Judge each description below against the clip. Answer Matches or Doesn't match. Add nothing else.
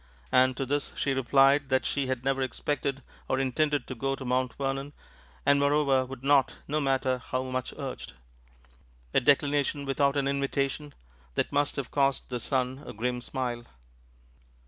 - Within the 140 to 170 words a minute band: Matches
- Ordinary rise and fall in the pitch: Doesn't match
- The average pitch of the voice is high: Doesn't match